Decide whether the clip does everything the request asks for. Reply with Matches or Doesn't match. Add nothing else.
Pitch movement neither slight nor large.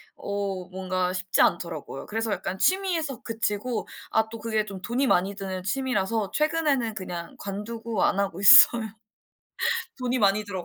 Matches